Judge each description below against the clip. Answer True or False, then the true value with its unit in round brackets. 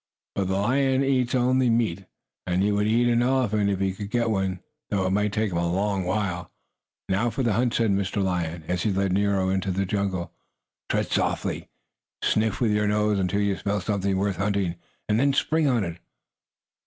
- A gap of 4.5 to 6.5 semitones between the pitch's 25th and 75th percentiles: False (3.1 semitones)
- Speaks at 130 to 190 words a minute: False (200 wpm)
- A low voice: True (100 Hz)